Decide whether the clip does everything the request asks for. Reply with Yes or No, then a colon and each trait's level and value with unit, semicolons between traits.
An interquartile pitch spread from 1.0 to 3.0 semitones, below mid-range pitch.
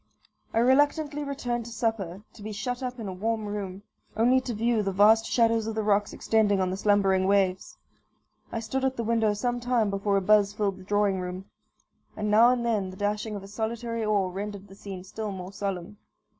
No: average, 2.7 semitones; high, 210 Hz